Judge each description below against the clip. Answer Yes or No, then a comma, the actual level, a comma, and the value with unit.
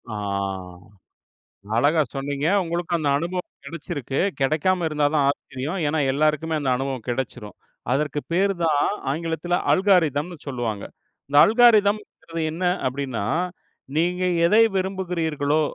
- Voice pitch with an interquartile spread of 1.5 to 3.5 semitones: No, average, 4.0 semitones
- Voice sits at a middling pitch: Yes, medium, 155 Hz